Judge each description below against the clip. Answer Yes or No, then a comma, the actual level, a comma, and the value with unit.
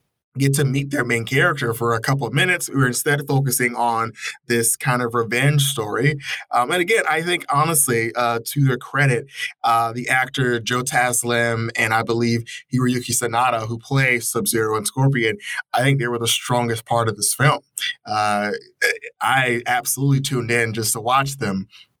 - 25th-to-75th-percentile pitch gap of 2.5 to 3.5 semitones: Yes, average, 3.0 semitones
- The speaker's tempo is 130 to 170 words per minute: No, average, 185 wpm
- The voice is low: Yes, low, 120 Hz